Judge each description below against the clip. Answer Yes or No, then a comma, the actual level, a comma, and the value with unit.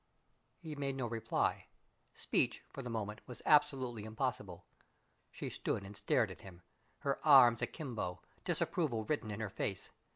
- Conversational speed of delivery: Yes, average, 150 wpm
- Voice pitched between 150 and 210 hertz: No, low, 120 Hz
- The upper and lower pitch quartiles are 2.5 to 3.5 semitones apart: No, average, 4.5 semitones